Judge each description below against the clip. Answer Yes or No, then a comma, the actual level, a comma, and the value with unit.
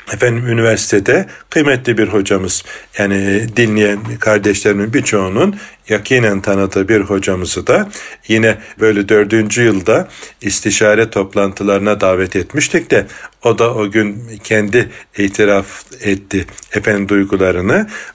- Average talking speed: Yes, average, 105 wpm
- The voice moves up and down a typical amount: No, narrow, 2.0 semitones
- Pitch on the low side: Yes, low, 105 Hz